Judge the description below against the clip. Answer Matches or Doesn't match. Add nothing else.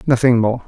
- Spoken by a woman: Doesn't match